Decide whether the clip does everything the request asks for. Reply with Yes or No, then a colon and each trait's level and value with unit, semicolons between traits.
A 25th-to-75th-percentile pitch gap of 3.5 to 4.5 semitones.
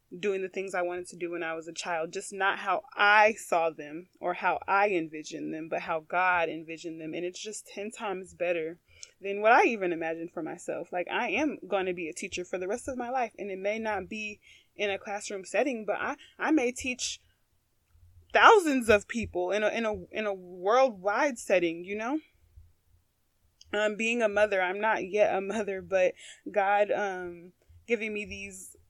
Yes: average, 4.1 semitones